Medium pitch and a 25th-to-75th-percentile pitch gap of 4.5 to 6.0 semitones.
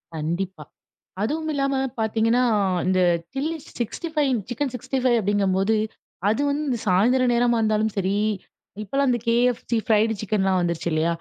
No: high, 225 Hz; average, 4.9 semitones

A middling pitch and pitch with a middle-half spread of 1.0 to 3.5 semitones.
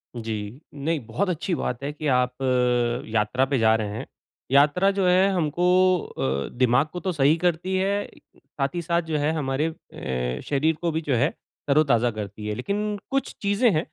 No: medium, 150 Hz; wide, 5.8 semitones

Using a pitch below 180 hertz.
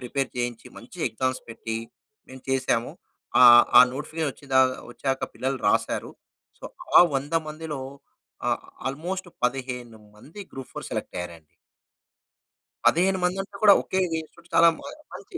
Yes: low, 135 Hz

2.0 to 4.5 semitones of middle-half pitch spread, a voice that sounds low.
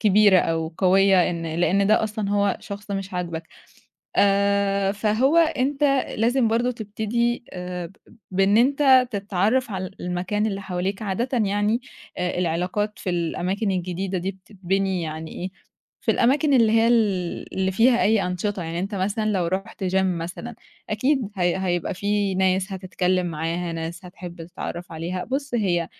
No: average, 3.2 semitones; high, 195 Hz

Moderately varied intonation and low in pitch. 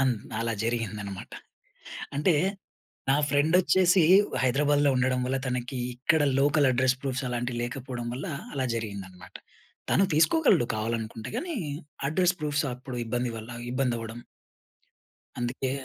Yes: average, 3.5 semitones; low, 130 Hz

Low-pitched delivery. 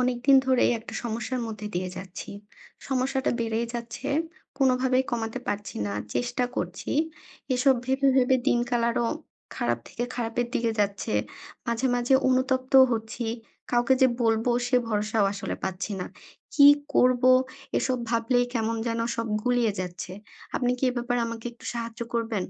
No: high, 240 Hz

